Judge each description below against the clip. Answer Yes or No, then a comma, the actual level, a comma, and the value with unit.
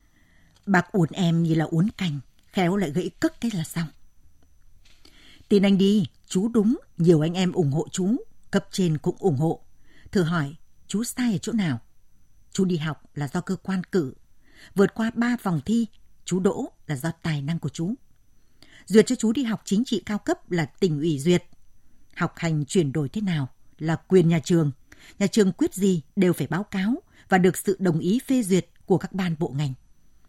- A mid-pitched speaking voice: Yes, medium, 180 Hz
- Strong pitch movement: No, average, 4.5 semitones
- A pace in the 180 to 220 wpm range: Yes, average, 200 wpm